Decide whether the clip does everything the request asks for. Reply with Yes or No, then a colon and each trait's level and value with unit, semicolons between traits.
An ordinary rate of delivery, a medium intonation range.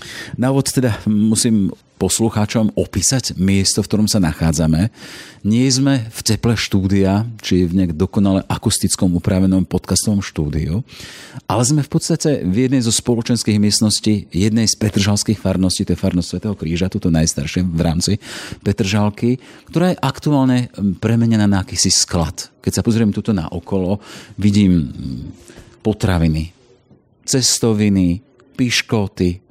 Yes: average, 130 wpm; average, 3.6 semitones